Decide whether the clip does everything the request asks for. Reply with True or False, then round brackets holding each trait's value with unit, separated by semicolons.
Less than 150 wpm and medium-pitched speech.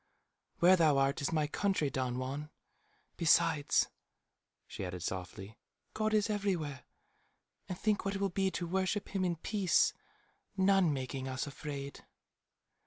True (140 wpm; 165 Hz)